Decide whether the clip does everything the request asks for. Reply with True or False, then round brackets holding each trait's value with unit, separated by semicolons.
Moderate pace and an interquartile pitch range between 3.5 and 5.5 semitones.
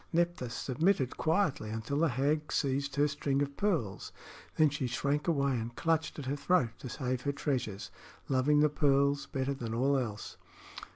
False (170 wpm; 2.7 semitones)